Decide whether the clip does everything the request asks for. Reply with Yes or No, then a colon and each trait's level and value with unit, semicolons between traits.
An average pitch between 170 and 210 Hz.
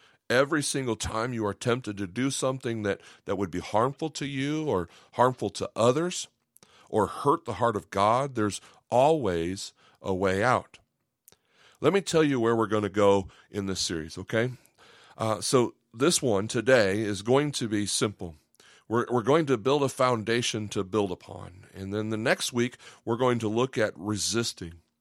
No: low, 110 Hz